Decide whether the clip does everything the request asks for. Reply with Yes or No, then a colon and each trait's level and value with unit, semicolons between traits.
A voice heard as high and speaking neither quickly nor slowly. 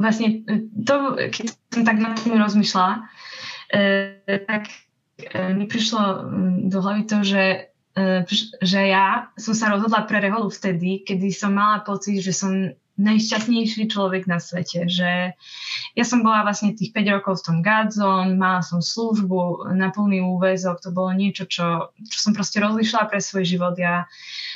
Yes: high, 200 Hz; average, 155 wpm